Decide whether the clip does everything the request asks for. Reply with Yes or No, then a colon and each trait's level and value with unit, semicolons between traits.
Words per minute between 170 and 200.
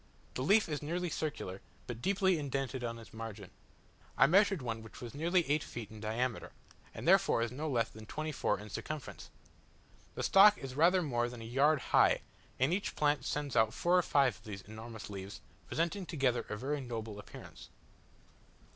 Yes: average, 180 wpm